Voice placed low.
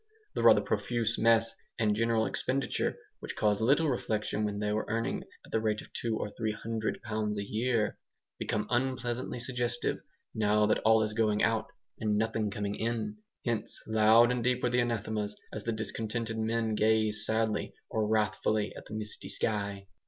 Yes: low, 110 Hz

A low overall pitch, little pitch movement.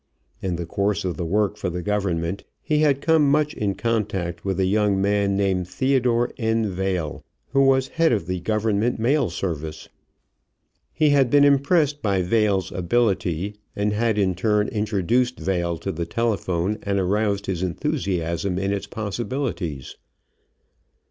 No: low, 100 Hz; average, 4.3 semitones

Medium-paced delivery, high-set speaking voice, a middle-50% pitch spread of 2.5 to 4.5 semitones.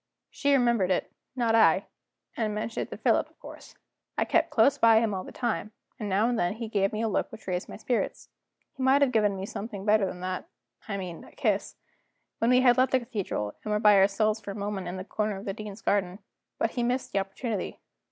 No: fast, 235 wpm; high, 210 Hz; average, 2.9 semitones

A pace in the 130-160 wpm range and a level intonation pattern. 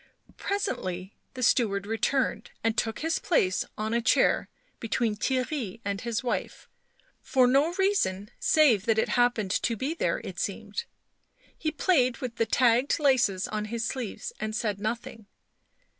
No: average, 150 wpm; average, 4.0 semitones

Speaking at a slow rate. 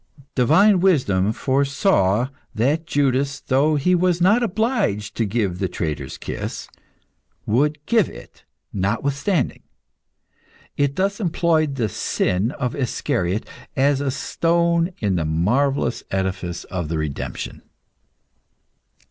Yes: slow, 115 wpm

